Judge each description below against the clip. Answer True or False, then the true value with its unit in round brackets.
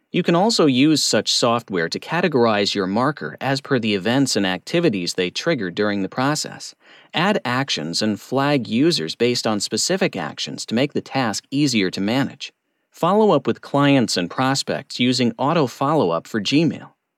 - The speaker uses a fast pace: False (170 wpm)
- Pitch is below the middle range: True (125 Hz)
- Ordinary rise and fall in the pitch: False (5.8 semitones)